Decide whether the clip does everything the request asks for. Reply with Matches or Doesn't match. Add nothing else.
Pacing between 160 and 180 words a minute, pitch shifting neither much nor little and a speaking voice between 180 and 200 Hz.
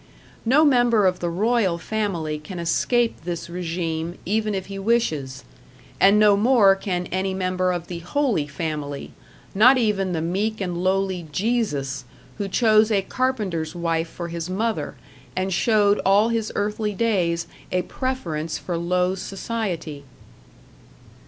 Doesn't match